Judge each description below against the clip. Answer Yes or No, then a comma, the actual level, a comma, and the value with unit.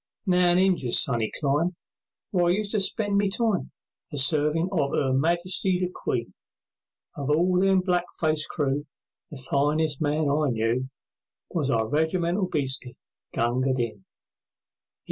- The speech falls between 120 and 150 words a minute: Yes, average, 140 wpm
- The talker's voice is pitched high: No, medium, 155 Hz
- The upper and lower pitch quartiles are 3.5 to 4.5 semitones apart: No, average, 5.0 semitones